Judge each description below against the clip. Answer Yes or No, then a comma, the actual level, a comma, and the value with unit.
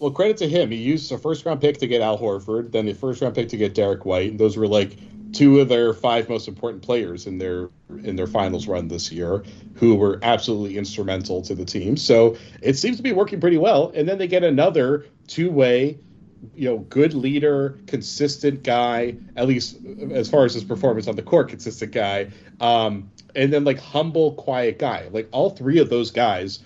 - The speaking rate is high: Yes, fast, 215 wpm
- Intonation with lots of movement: Yes, wide, 5.7 semitones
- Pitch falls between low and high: No, low, 120 Hz